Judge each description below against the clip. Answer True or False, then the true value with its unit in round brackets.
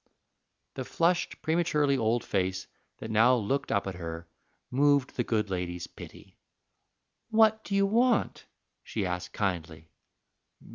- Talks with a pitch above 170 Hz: False (115 Hz)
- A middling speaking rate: False (130 wpm)